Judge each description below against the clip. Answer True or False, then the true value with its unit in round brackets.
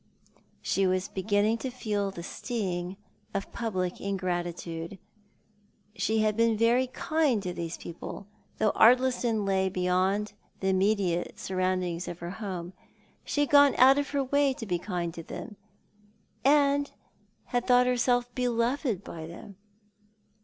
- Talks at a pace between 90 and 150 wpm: True (140 wpm)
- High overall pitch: True (205 Hz)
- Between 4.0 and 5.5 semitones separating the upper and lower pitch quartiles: True (5.1 semitones)